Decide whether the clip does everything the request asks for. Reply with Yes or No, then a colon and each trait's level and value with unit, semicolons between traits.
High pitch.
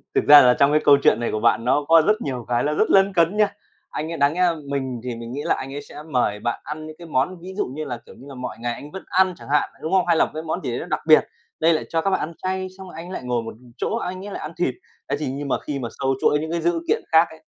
No: medium, 150 Hz